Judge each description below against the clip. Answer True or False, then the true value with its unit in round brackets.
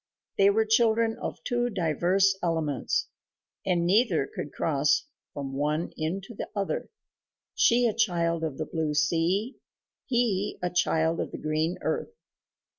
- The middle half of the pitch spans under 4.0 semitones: False (5.3 semitones)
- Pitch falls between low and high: True (175 Hz)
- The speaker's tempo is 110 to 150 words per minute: True (140 wpm)